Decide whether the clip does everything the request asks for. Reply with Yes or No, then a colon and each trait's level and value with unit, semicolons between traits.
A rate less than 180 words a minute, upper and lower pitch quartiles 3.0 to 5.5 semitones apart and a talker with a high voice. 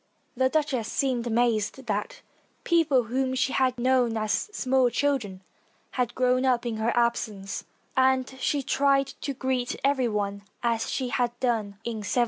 No: average, 160 wpm; narrow, 2.5 semitones; very high, 250 Hz